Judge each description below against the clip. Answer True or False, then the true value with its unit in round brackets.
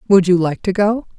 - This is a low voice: False (190 Hz)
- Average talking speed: False (255 wpm)